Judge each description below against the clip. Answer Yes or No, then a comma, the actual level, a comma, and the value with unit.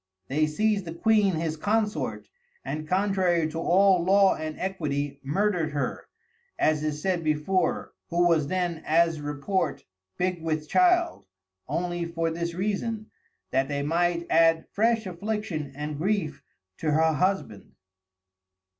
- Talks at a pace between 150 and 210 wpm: No, slow, 135 wpm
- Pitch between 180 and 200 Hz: No, medium, 170 Hz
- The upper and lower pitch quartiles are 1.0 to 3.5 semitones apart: No, average, 3.9 semitones